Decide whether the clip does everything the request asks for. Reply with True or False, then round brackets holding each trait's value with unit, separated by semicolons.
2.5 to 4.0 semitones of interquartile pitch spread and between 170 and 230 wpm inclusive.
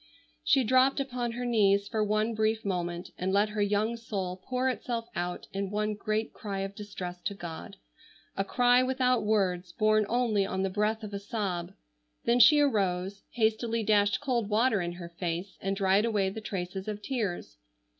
True (3.1 semitones; 180 wpm)